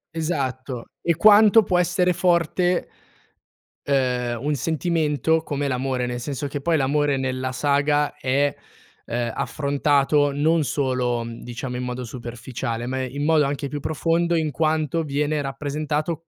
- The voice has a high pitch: No, medium, 145 Hz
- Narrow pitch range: No, average, 3.5 semitones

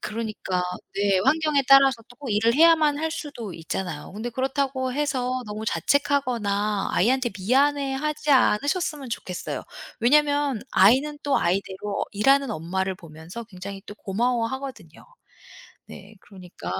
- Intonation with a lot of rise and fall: Yes, wide, 5.9 semitones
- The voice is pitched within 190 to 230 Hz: No, high, 240 Hz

